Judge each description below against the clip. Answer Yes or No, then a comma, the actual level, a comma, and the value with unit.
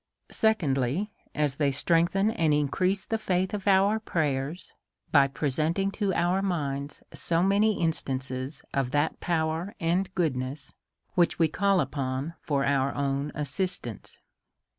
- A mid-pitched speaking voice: Yes, medium, 160 Hz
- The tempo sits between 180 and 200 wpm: No, slow, 135 wpm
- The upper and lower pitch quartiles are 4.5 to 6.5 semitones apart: Yes, wide, 5.4 semitones